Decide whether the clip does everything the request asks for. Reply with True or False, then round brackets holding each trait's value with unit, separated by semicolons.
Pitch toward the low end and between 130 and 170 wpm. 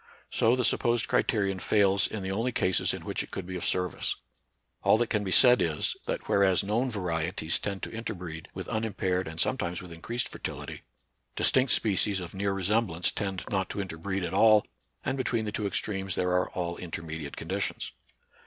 False (95 Hz; 190 wpm)